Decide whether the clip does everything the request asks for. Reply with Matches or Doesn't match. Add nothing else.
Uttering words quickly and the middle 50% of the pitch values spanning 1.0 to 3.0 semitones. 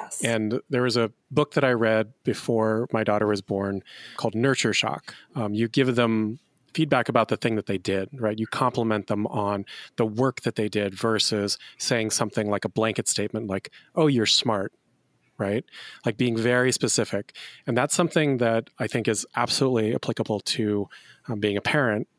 Doesn't match